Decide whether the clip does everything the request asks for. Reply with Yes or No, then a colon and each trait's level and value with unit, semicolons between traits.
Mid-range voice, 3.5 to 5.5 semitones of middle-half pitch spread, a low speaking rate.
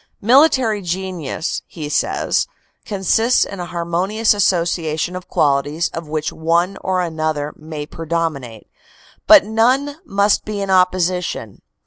Yes: medium, 175 Hz; average, 4.1 semitones; slow, 125 wpm